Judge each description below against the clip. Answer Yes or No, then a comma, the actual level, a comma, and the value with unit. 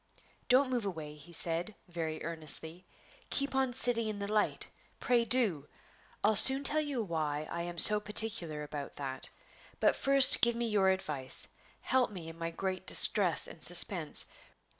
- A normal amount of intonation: No, wide, 6.4 semitones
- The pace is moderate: Yes, average, 160 wpm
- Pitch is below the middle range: No, high, 190 Hz